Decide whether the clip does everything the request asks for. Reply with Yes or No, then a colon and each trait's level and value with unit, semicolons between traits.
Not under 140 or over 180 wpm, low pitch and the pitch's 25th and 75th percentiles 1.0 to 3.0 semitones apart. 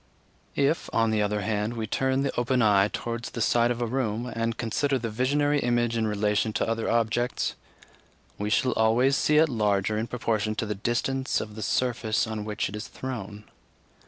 No: average, 190 wpm; low, 115 Hz; narrow, 2.6 semitones